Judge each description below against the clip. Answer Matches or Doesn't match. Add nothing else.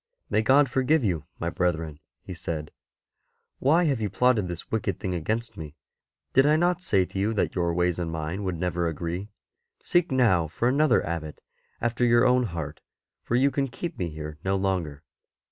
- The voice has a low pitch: Matches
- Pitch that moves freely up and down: Matches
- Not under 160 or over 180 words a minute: Doesn't match